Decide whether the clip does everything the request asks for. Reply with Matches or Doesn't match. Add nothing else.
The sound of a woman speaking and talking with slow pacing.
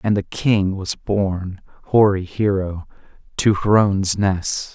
Doesn't match